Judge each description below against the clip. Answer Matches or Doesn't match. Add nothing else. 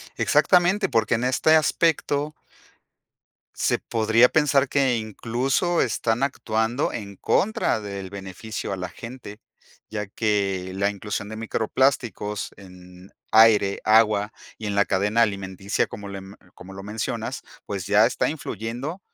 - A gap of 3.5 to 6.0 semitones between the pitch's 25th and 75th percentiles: Matches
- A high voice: Doesn't match